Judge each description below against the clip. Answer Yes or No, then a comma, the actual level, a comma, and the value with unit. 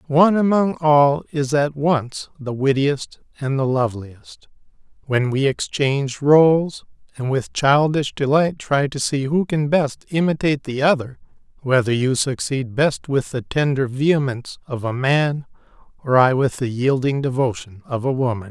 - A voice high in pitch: No, medium, 140 Hz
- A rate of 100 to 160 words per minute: Yes, average, 155 wpm